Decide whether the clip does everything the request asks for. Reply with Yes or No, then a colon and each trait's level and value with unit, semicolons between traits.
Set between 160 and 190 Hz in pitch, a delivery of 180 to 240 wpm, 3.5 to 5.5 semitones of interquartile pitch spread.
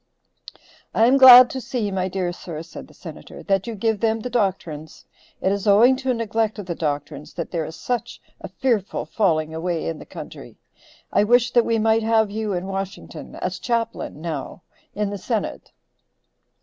No: high, 205 Hz; average, 190 wpm; average, 4.6 semitones